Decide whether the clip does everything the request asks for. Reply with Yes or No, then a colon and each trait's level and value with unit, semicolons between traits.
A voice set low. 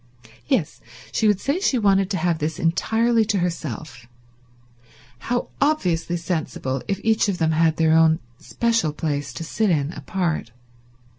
No: medium, 170 Hz